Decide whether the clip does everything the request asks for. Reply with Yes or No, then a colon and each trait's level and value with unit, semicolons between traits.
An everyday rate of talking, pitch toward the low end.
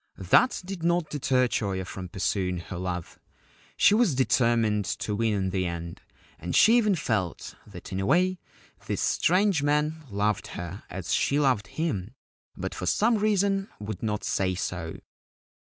Yes: average, 160 wpm; low, 110 Hz